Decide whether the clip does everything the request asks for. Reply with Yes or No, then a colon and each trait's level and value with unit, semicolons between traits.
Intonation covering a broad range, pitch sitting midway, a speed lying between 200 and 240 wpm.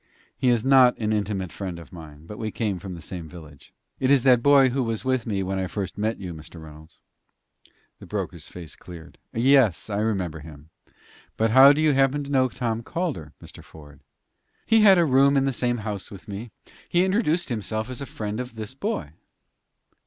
No: wide, 6.7 semitones; low, 110 Hz; fast, 205 wpm